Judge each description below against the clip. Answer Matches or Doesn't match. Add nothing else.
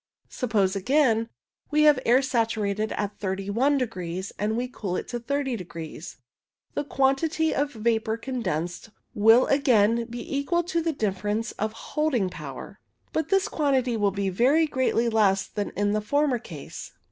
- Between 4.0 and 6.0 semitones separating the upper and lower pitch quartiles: Matches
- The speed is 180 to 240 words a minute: Doesn't match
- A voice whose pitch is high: Matches